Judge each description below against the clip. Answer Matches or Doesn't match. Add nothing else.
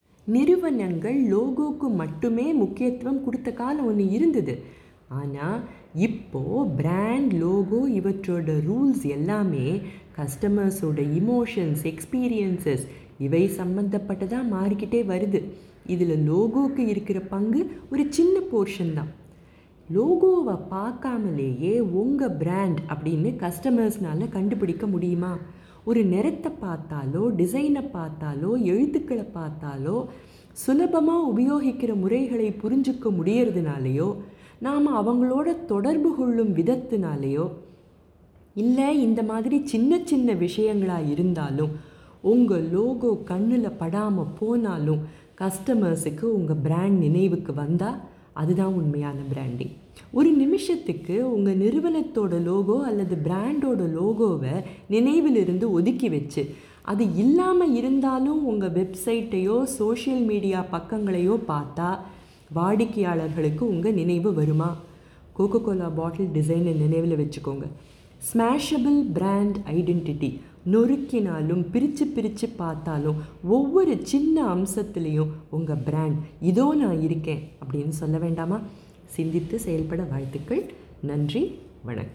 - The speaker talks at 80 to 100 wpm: Matches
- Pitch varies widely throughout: Matches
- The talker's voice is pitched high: Matches